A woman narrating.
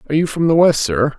No: male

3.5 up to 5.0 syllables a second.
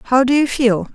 Yes: 4.5 syllables/s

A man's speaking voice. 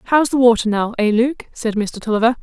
No: female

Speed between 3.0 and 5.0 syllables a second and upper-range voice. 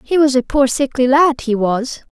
Yes: 4.7 syllables/s; very high, 265 Hz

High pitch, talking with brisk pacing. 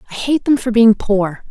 Yes: high, 225 Hz; fast, 240 wpm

